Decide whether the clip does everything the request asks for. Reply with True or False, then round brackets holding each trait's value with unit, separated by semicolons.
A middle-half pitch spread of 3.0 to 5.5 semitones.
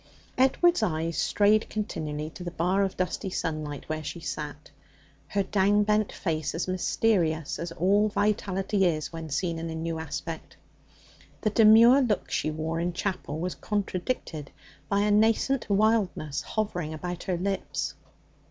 True (4.5 semitones)